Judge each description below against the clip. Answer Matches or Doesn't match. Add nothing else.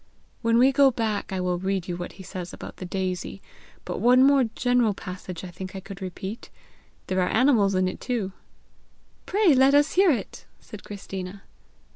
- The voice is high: Matches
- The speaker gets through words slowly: Doesn't match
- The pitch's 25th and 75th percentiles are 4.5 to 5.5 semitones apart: Matches